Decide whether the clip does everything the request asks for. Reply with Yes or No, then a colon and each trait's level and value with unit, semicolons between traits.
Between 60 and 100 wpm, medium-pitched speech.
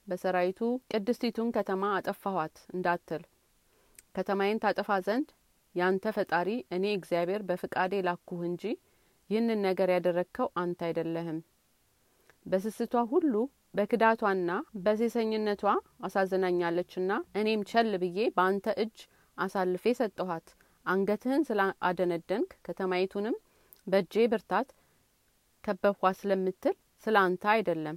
No: average, 90 wpm; high, 195 Hz